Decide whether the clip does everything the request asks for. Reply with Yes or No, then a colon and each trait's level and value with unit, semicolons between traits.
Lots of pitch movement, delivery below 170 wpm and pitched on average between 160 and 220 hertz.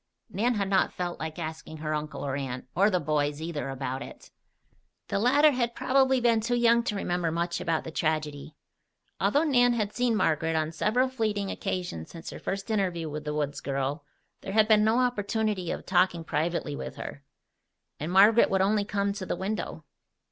No: wide, 5.7 semitones; average, 190 wpm; medium, 185 Hz